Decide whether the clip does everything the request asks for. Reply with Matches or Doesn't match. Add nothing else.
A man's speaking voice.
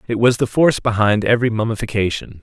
Matches